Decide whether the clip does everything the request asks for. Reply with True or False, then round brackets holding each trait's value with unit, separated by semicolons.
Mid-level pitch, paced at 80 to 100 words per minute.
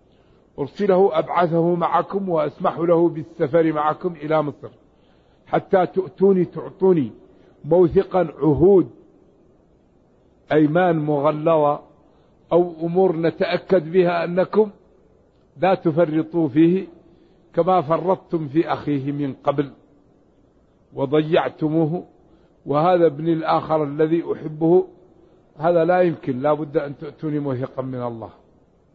True (165 Hz; 95 wpm)